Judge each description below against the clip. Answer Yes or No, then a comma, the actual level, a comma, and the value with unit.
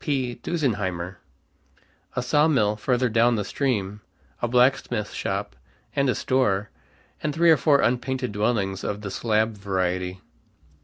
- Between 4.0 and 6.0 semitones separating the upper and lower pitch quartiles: Yes, average, 4.5 semitones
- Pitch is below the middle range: Yes, low, 115 Hz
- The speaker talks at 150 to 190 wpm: No, slow, 135 wpm